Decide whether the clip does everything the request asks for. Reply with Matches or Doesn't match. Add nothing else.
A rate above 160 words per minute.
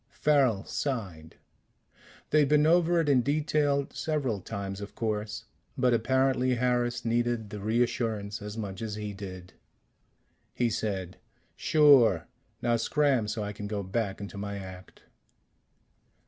Doesn't match